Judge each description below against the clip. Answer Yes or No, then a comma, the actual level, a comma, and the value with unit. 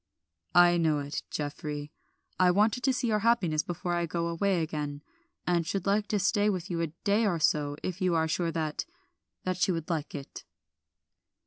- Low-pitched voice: No, medium, 175 Hz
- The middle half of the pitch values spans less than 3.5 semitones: No, average, 4.0 semitones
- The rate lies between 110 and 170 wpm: No, average, 190 wpm